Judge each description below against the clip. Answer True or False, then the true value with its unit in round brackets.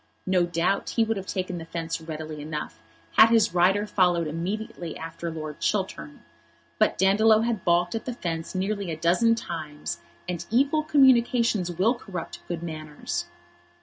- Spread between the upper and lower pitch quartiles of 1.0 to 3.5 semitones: False (4.9 semitones)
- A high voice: False (175 Hz)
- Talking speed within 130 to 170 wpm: True (155 wpm)